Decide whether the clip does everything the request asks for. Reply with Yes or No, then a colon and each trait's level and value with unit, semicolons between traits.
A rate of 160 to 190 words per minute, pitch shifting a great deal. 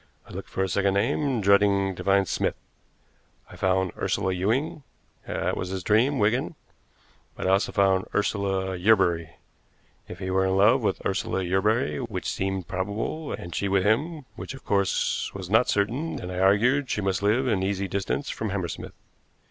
No: average, 180 wpm; average, 2.7 semitones